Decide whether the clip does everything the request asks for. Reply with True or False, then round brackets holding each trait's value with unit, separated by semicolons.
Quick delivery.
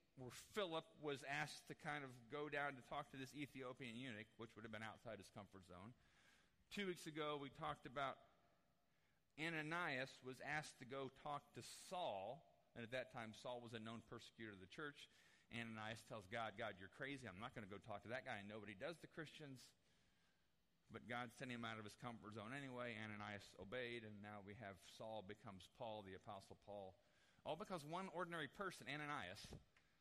False (195 wpm)